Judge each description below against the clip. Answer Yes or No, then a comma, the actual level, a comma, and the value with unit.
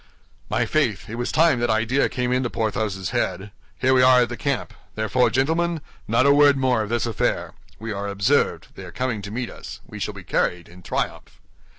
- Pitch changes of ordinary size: Yes, average, 3.2 semitones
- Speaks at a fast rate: Yes, fast, 210 wpm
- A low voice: Yes, low, 120 Hz